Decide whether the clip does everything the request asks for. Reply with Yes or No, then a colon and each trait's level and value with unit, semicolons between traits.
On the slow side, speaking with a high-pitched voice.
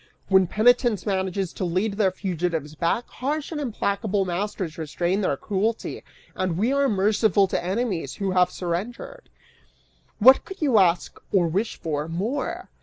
No: average, 150 wpm; high, 195 Hz